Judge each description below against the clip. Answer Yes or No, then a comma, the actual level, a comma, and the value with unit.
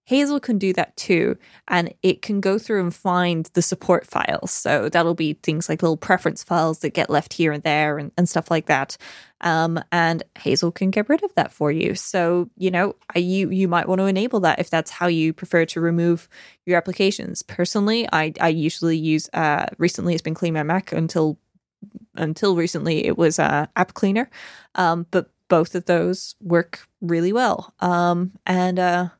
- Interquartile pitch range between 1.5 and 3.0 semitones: Yes, narrow, 2.4 semitones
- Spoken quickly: No, average, 195 wpm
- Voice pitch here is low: No, medium, 175 Hz